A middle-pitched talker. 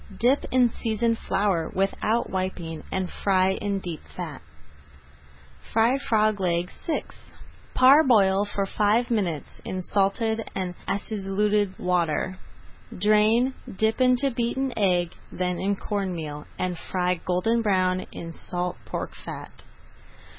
No: high, 195 Hz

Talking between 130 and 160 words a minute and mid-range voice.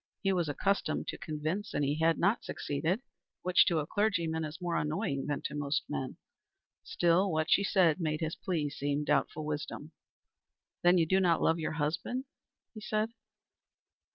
No: average, 170 wpm; medium, 165 Hz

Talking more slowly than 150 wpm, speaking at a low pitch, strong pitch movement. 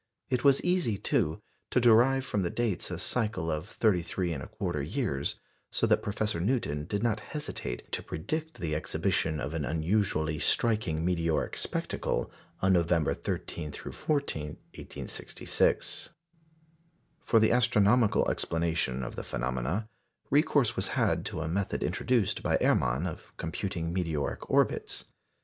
Yes: slow, 135 wpm; very low, 90 Hz; wide, 6.3 semitones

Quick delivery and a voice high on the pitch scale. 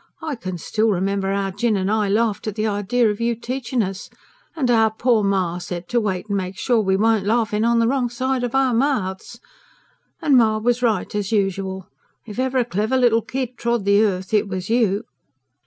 Yes: fast, 210 wpm; high, 220 Hz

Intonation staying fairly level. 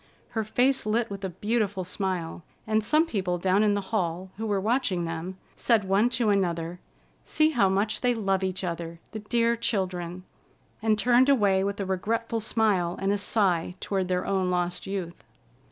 No: average, 3.3 semitones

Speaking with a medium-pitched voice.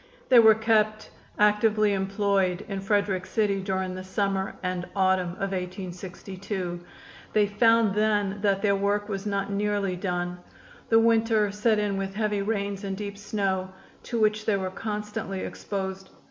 No: high, 200 Hz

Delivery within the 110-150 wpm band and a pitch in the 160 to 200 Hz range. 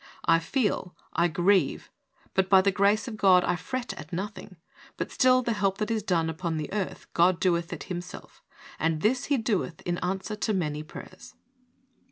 No: average, 185 wpm; high, 190 Hz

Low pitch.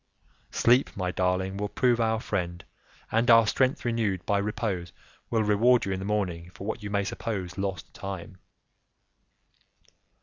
Yes: low, 100 Hz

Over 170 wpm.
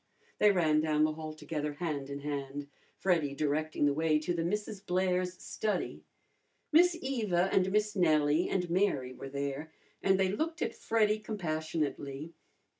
No: average, 155 wpm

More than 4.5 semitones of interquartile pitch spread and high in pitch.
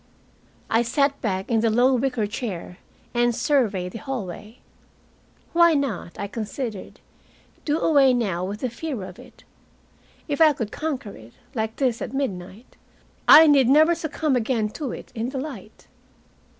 Yes: average, 4.9 semitones; high, 240 Hz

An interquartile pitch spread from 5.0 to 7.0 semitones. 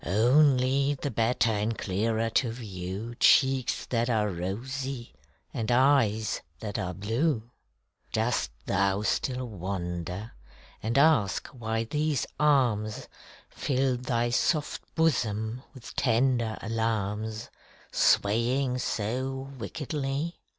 No: average, 3.6 semitones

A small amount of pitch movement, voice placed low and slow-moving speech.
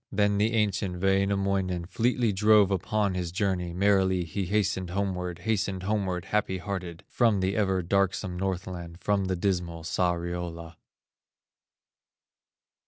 Yes: narrow, 2.2 semitones; very low, 95 Hz; slow, 120 wpm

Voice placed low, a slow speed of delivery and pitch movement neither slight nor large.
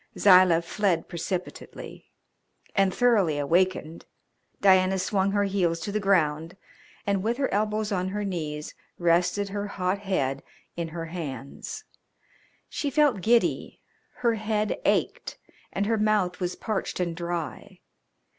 No: high, 190 Hz; slow, 130 wpm; average, 3.3 semitones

